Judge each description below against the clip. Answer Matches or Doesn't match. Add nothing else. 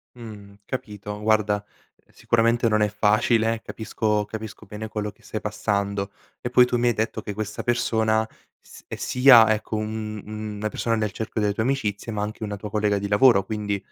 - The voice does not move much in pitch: Matches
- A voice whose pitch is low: Matches